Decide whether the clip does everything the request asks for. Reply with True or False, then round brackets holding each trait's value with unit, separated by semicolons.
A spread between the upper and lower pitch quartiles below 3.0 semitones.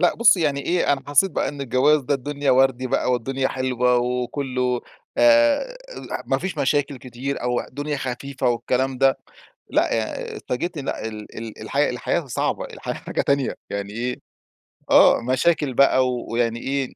True (2.5 semitones)